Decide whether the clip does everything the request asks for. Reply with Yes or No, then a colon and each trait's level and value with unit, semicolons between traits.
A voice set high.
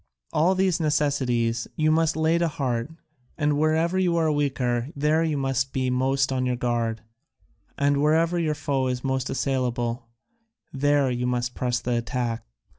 No: low, 135 Hz